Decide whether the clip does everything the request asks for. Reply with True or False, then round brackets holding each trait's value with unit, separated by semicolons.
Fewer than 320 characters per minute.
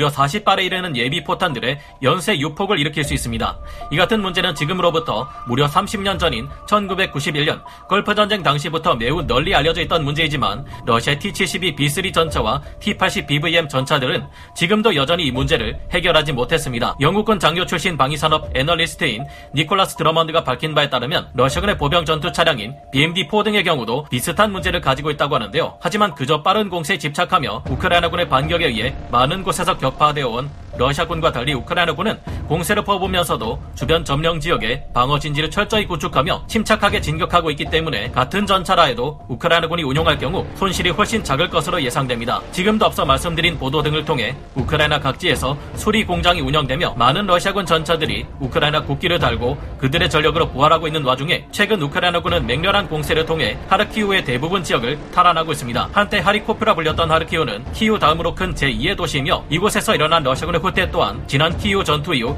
False (430 characters per minute)